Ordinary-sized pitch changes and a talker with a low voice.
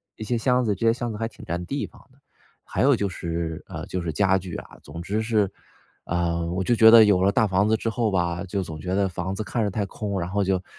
Yes: average, 3.8 semitones; low, 100 Hz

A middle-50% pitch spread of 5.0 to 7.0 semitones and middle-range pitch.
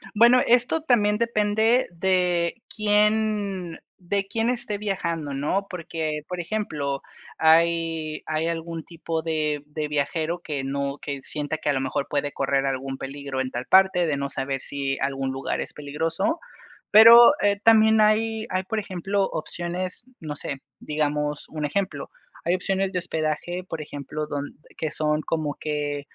Yes: wide, 5.4 semitones; medium, 165 Hz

